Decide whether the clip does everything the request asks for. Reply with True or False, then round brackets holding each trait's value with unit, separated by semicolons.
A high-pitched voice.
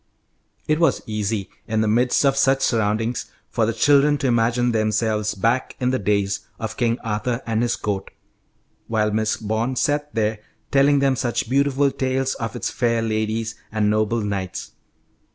False (115 Hz)